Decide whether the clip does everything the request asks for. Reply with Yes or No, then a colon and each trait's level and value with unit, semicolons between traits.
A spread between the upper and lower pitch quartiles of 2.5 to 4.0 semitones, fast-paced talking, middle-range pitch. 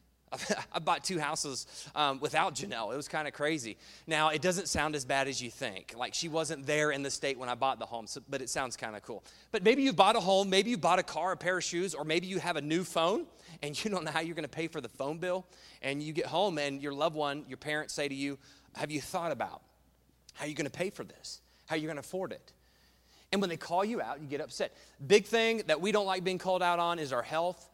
No: average, 4.7 semitones; fast, 275 wpm; medium, 155 Hz